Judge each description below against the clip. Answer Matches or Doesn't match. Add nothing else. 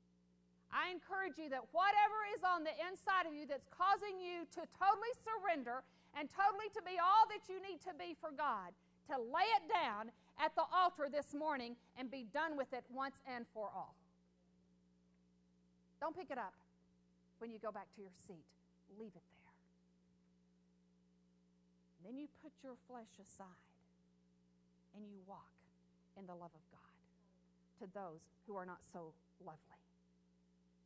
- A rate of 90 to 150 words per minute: Doesn't match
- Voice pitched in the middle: Doesn't match